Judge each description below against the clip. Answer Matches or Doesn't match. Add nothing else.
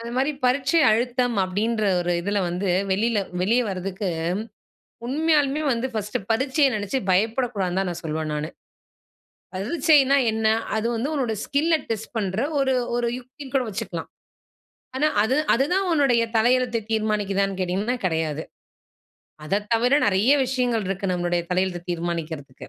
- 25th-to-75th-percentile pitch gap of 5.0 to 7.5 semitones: Matches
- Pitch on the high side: Matches